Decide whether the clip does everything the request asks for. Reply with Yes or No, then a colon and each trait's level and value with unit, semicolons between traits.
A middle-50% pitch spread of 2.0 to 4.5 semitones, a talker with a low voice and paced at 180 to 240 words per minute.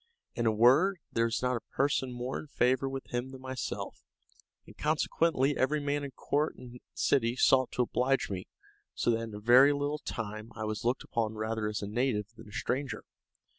Yes: average, 3.2 semitones; low, 125 Hz; average, 200 wpm